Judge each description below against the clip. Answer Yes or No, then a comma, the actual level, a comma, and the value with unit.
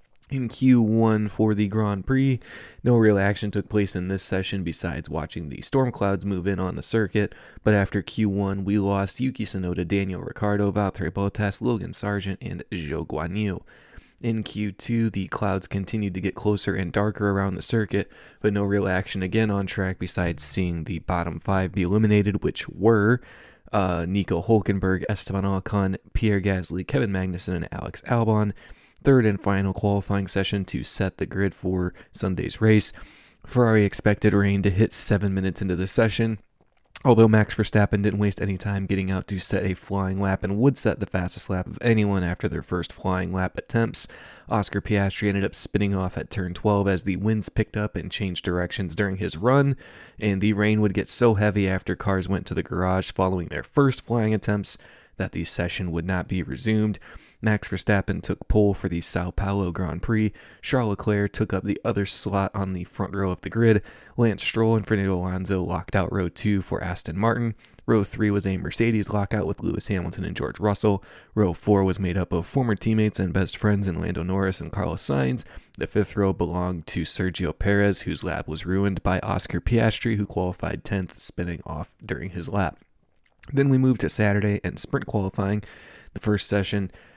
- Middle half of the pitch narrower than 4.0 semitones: Yes, narrow, 2.4 semitones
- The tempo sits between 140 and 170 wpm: No, average, 190 wpm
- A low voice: Yes, low, 100 Hz